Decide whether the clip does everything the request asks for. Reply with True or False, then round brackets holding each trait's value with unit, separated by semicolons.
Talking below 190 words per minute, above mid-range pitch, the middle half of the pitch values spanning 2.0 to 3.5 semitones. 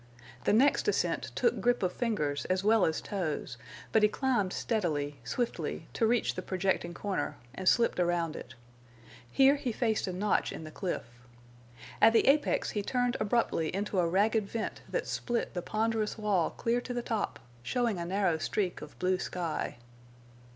False (170 wpm; 205 Hz; 4.7 semitones)